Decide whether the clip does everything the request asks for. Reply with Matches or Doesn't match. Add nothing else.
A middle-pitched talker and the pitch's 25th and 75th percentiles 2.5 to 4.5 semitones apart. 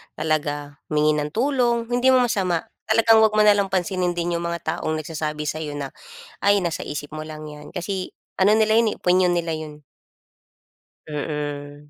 Doesn't match